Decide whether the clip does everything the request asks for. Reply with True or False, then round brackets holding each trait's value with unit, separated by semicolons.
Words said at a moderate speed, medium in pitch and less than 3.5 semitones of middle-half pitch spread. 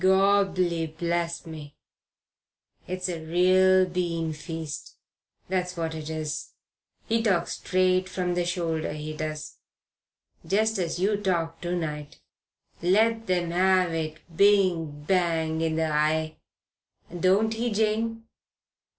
False (120 wpm; 175 Hz; 2.8 semitones)